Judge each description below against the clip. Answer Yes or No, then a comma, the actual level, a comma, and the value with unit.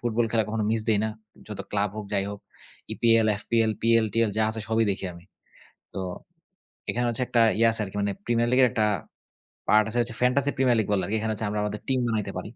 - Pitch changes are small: Yes, narrow, 1.9 semitones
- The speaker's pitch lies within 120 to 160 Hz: No, low, 110 Hz